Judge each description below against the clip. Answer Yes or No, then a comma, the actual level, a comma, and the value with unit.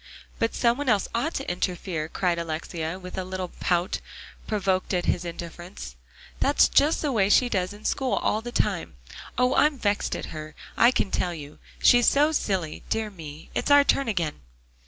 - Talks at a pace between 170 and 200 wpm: Yes, average, 185 wpm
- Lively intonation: Yes, wide, 5.9 semitones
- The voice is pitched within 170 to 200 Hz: Yes, high, 190 Hz